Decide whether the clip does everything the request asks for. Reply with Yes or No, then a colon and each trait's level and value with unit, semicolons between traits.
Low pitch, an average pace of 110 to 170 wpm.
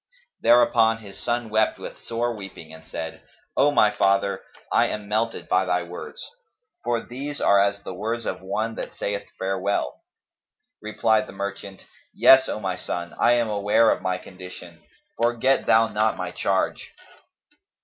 Yes: low, 105 Hz; average, 160 wpm